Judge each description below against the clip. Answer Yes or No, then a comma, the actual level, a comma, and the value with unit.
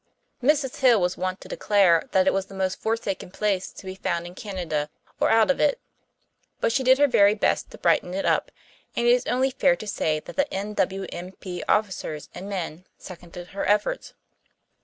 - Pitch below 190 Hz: No, high, 195 Hz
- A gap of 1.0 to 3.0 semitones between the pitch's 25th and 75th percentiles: No, average, 4.1 semitones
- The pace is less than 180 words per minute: No, average, 195 wpm